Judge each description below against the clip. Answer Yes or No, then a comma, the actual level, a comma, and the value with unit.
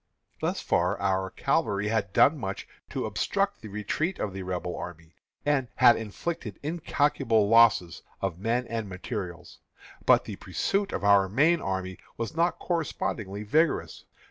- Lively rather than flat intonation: Yes, wide, 7.0 semitones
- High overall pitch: No, low, 105 Hz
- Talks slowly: No, average, 145 wpm